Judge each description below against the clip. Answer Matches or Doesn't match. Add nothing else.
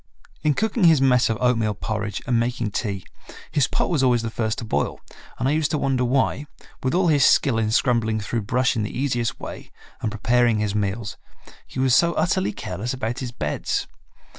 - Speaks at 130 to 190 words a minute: Doesn't match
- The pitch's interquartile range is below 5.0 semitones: Matches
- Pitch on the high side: Doesn't match